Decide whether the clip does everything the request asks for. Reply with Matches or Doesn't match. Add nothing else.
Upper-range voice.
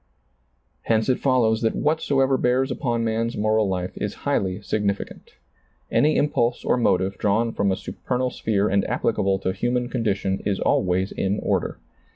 Doesn't match